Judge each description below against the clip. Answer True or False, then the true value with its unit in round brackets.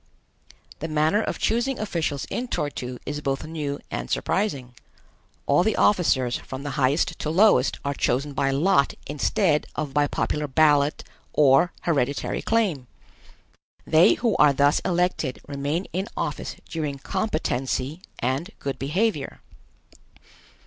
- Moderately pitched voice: True (150 Hz)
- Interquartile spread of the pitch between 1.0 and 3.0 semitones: False (4.4 semitones)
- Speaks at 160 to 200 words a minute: False (135 wpm)